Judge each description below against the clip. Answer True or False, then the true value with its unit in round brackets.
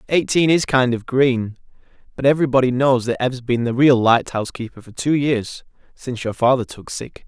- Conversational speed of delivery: True (190 wpm)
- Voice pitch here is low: True (125 Hz)